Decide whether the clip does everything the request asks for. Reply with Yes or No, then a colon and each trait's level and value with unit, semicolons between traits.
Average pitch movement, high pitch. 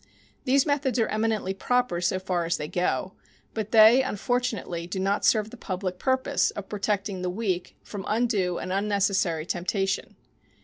Yes: average, 3.5 semitones; high, 200 Hz